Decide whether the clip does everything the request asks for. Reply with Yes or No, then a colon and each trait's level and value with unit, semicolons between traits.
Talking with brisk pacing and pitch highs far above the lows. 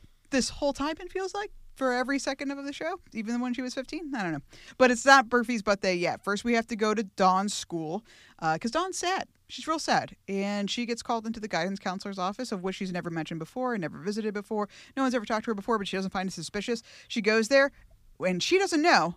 Yes: fast, 250 wpm; wide, 5.7 semitones